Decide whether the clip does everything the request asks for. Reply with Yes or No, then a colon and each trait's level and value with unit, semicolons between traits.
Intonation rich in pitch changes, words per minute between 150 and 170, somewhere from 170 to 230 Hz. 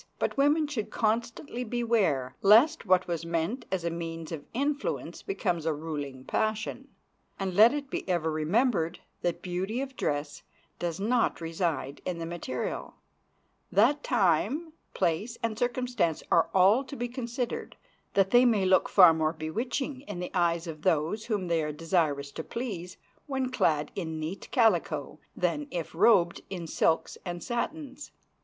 Yes: wide, 6.7 semitones; average, 155 wpm; medium, 185 Hz